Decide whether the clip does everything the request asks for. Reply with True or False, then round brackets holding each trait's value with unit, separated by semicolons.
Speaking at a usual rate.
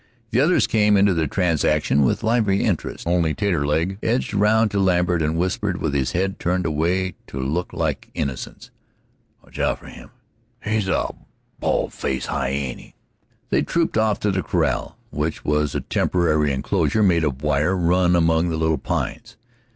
True (165 wpm)